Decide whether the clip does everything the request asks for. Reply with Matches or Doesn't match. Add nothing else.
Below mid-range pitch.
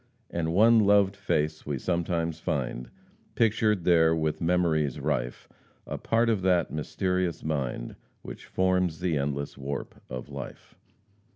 Matches